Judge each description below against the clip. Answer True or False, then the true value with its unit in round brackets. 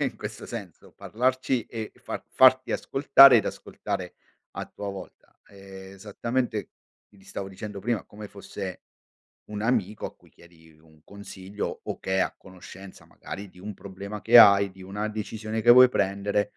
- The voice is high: False (100 Hz)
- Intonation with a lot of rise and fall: False (2.5 semitones)